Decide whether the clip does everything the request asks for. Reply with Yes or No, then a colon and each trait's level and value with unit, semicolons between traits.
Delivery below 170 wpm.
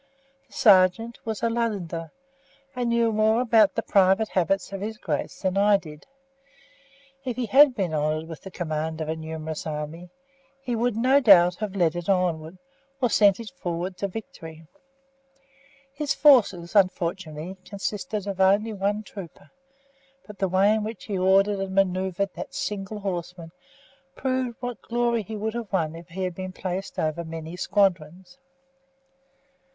Yes: average, 160 wpm